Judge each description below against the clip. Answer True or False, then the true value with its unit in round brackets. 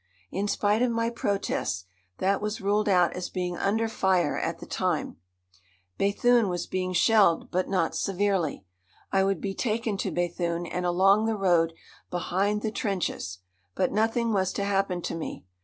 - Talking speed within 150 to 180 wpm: True (165 wpm)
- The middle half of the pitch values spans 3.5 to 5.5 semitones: False (2.9 semitones)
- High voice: True (195 Hz)